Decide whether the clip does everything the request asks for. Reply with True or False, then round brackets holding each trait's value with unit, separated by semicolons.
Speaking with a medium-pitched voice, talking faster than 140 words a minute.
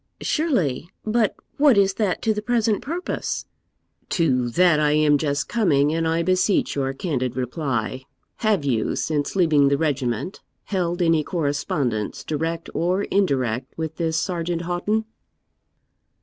False (165 Hz; 135 wpm)